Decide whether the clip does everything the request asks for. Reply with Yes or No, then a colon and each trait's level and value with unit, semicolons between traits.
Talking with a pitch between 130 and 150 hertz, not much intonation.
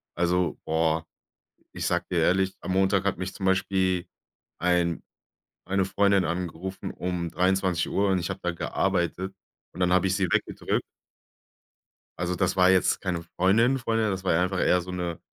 No: very low, 90 Hz; narrow, 1.5 semitones